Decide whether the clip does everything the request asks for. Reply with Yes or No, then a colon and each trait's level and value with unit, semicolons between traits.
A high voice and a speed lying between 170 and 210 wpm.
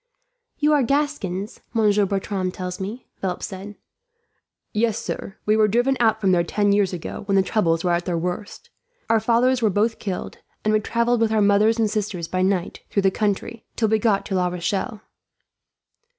Yes: high, 205 Hz; average, 190 wpm